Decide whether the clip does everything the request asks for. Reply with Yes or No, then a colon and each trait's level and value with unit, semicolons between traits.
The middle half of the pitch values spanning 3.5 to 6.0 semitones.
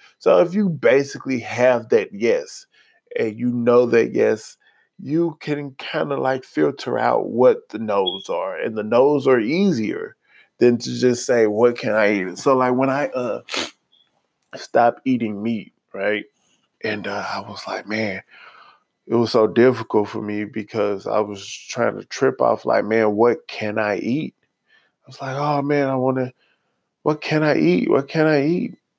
Yes: average, 5.0 semitones